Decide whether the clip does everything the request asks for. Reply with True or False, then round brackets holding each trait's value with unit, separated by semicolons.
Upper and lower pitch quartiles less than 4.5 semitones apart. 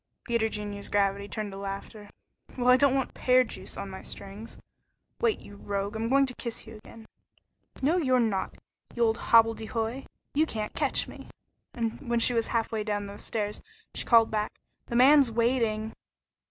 True (3.0 semitones)